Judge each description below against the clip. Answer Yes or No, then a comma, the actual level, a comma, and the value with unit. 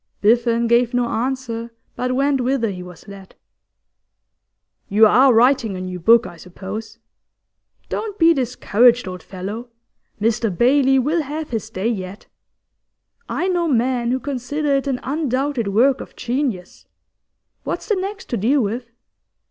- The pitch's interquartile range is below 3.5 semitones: No, average, 3.9 semitones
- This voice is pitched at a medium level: No, high, 240 Hz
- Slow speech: No, average, 145 wpm